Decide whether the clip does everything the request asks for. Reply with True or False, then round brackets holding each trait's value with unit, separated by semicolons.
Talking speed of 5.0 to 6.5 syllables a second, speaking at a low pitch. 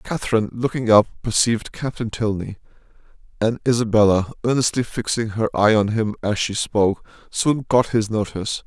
True (5.4 syllables/s; 110 Hz)